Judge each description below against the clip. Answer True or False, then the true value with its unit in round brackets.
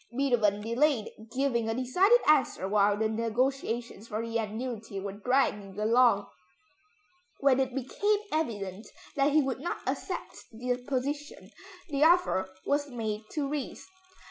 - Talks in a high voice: True (245 Hz)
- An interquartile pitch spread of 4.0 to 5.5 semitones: True (4.4 semitones)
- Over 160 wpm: False (135 wpm)